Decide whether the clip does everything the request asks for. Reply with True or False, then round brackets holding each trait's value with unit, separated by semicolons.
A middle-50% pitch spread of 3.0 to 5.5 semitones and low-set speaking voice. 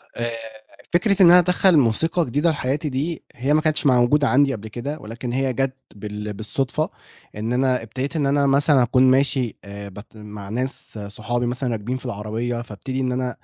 True (4.0 semitones; 130 Hz)